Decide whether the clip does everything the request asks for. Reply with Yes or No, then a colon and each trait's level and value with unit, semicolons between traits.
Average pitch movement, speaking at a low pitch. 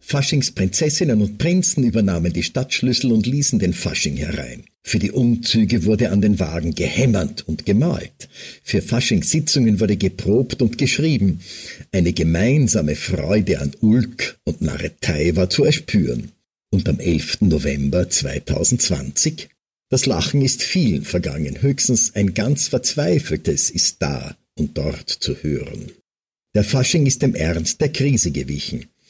No: wide, 7.4 semitones; low, 110 Hz